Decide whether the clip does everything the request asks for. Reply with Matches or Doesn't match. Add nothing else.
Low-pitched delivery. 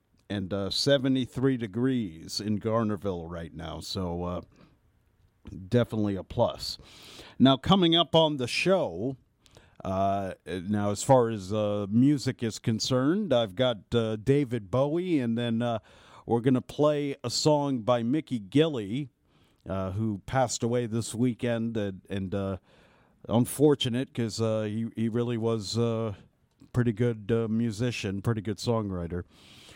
Matches